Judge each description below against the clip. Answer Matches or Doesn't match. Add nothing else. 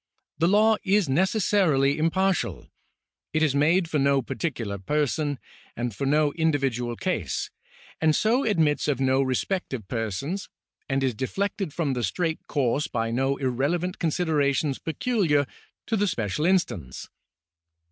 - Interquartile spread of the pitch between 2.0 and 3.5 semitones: Doesn't match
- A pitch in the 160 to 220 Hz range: Doesn't match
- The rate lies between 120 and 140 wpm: Matches